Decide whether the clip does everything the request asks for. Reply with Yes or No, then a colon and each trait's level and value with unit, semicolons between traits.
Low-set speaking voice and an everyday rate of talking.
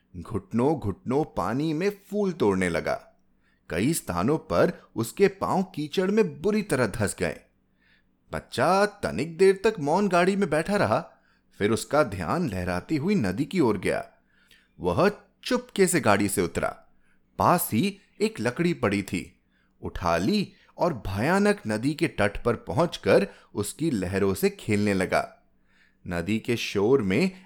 No: medium, 155 Hz; average, 145 wpm